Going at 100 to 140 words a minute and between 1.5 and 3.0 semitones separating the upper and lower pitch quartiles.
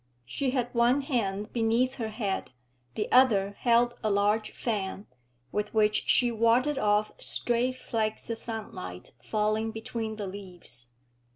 Yes: slow, 135 wpm; narrow, 2.6 semitones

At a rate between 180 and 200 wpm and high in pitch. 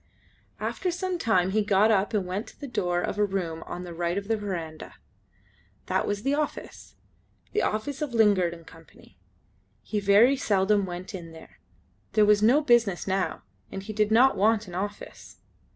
Yes: average, 185 wpm; high, 205 Hz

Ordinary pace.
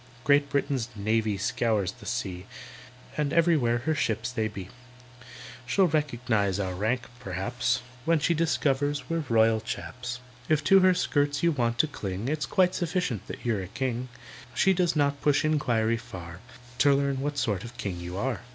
Yes: average, 170 wpm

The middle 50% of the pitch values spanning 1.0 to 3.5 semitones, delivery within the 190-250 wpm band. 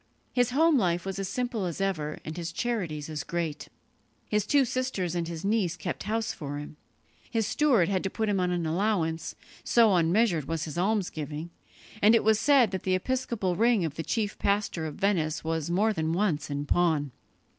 No: average, 5.2 semitones; average, 195 wpm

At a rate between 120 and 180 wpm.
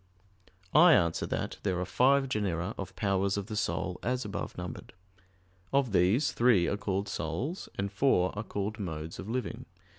Yes: average, 170 wpm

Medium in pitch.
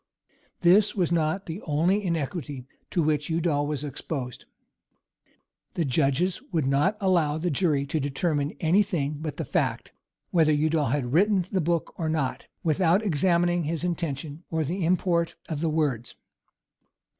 Yes: medium, 160 Hz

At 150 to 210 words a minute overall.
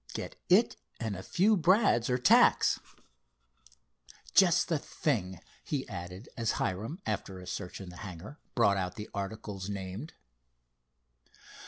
No: slow, 135 wpm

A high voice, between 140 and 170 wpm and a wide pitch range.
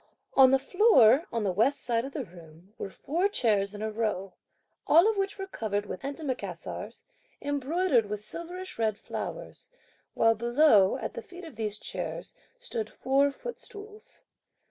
Yes: very high, 260 Hz; average, 160 wpm; wide, 8.3 semitones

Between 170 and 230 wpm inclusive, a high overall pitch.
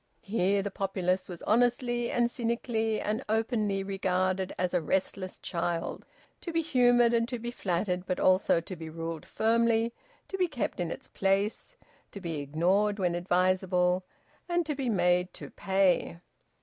No: average, 160 wpm; high, 195 Hz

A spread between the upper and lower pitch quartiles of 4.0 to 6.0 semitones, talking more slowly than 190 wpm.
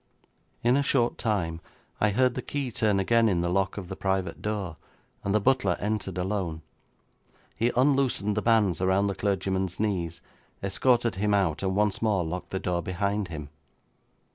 No: average, 2.8 semitones; average, 170 wpm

